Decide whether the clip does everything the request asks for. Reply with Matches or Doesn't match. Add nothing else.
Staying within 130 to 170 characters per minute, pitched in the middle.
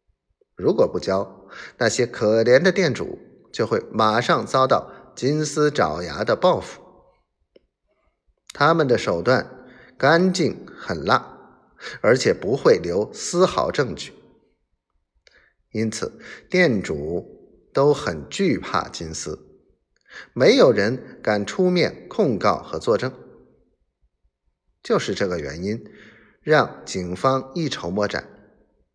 Doesn't match